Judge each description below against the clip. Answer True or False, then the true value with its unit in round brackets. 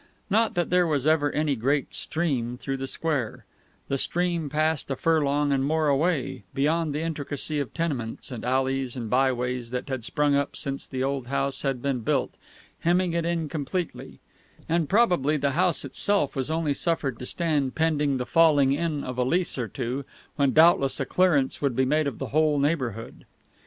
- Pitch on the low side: False (145 Hz)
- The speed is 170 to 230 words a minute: True (185 wpm)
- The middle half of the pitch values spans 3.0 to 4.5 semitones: True (3.4 semitones)